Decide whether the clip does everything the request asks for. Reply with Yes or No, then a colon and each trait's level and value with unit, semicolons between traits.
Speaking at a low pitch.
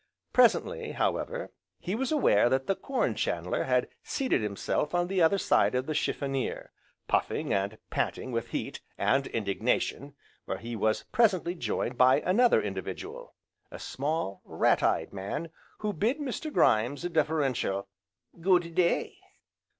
No: medium, 155 Hz